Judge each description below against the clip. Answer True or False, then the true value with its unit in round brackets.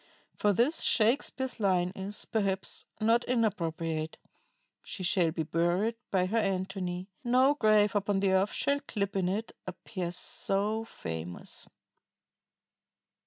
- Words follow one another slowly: True (125 wpm)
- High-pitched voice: True (195 Hz)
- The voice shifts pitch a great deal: False (3.5 semitones)